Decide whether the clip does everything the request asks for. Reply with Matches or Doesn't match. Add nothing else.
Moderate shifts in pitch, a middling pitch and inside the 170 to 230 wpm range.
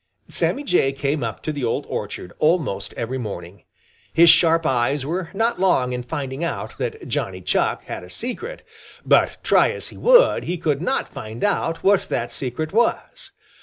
Doesn't match